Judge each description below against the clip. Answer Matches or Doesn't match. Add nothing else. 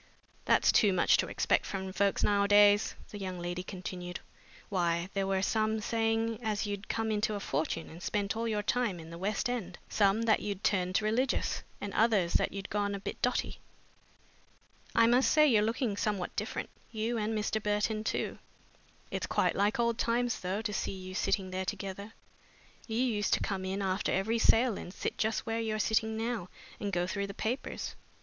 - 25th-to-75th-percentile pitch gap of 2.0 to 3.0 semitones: Matches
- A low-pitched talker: Doesn't match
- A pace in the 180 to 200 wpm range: Matches